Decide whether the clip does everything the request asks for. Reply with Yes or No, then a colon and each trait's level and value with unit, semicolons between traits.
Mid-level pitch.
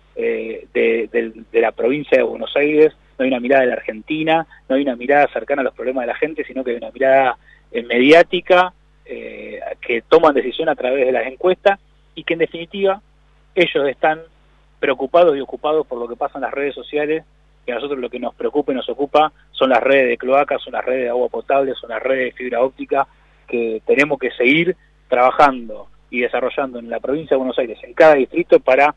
Yes: medium, 155 Hz